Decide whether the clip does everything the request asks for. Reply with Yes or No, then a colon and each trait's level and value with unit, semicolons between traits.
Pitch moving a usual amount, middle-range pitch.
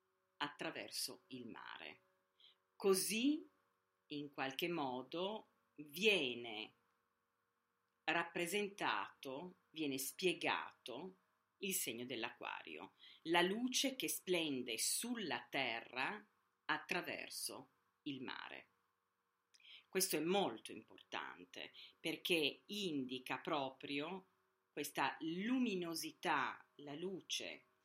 No: wide, 5.8 semitones; medium, 175 Hz